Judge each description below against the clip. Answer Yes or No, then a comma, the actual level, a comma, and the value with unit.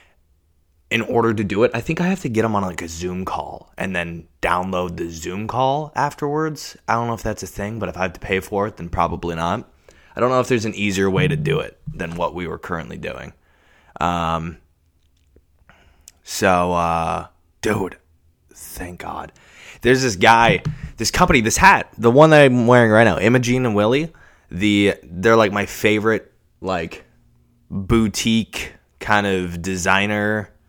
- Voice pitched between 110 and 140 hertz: No, very low, 95 Hz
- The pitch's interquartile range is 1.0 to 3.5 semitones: No, average, 5.2 semitones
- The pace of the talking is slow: No, average, 175 wpm